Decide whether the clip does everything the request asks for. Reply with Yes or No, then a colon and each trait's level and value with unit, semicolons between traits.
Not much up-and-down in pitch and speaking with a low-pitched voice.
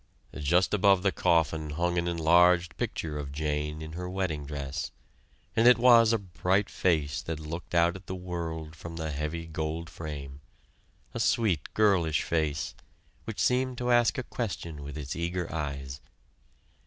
No: average, 3.3 semitones; very low, 85 Hz